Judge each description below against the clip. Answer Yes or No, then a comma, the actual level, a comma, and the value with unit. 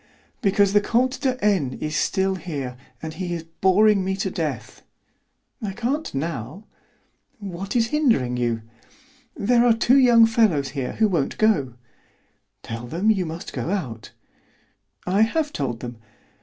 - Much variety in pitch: Yes, wide, 7.6 semitones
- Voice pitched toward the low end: No, high, 190 Hz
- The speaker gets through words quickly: No, average, 155 wpm